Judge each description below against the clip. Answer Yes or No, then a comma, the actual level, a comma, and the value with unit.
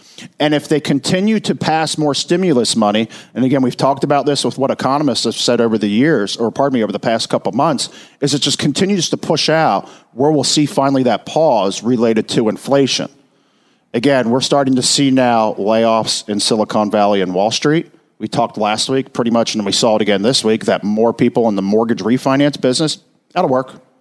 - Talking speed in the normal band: No, fast, 210 wpm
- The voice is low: Yes, low, 130 Hz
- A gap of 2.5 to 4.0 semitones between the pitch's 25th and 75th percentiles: No, average, 4.7 semitones